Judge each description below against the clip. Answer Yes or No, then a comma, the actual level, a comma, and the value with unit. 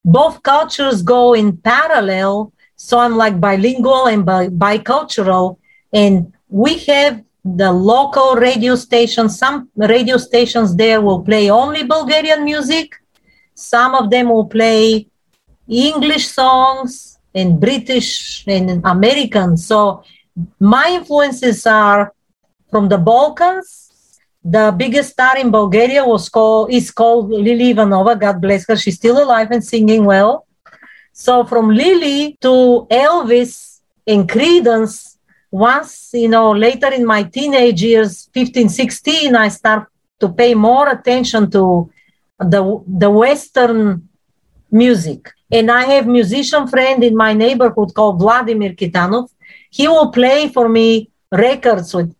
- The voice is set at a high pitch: Yes, high, 230 Hz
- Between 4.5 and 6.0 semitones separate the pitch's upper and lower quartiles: No, average, 3.8 semitones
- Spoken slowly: Yes, slow, 130 wpm